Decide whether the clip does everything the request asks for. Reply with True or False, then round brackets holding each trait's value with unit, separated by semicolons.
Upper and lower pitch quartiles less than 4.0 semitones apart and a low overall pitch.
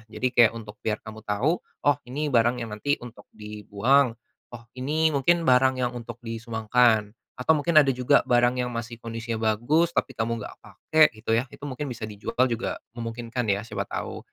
True (2.8 semitones; 120 Hz)